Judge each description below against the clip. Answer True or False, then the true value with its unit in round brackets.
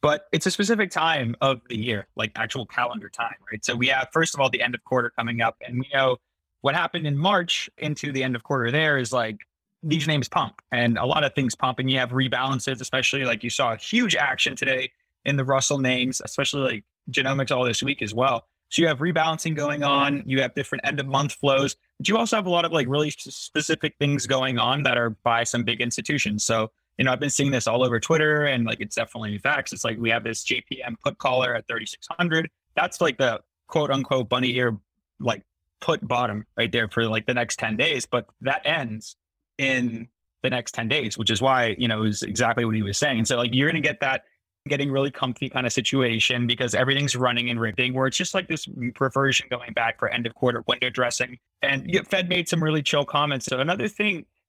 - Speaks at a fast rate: True (230 wpm)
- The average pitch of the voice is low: True (130 Hz)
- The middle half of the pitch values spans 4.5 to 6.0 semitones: False (3.5 semitones)